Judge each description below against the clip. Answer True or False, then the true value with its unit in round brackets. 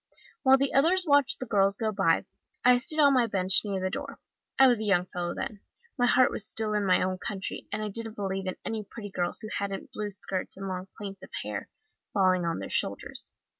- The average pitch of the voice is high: True (205 Hz)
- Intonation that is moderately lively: True (3.9 semitones)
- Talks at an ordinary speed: False (225 wpm)